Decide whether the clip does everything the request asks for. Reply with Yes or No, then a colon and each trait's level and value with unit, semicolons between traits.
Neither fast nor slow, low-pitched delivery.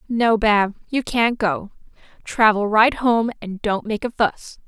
No: average, 165 wpm; high, 220 Hz